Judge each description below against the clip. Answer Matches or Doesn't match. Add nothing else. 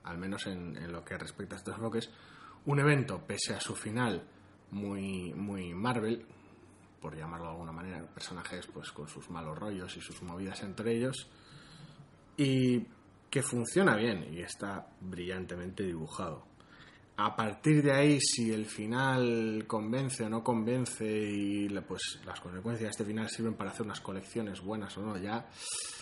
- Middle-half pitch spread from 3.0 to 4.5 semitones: Matches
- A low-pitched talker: Matches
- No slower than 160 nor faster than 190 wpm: Matches